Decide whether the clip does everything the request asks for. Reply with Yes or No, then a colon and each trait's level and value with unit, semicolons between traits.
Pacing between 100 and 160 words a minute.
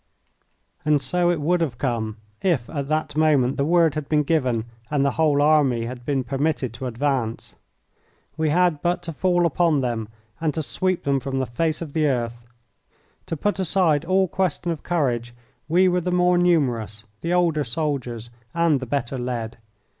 No: average, 180 wpm